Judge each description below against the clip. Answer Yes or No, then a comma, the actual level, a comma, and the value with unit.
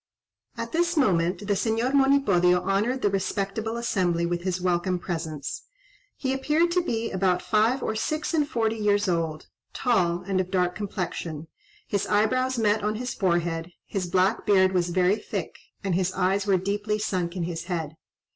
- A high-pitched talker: Yes, high, 195 Hz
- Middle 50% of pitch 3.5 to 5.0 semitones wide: Yes, average, 3.9 semitones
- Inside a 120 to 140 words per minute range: No, average, 170 wpm